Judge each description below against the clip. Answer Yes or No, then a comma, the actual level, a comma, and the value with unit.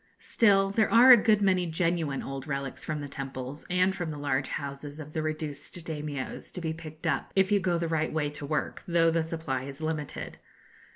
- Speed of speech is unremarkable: No, fast, 210 wpm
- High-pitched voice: No, medium, 160 Hz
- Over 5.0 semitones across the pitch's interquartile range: No, average, 3.6 semitones